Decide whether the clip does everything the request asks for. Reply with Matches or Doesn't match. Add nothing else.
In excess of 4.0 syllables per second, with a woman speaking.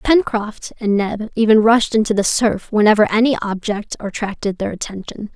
Matches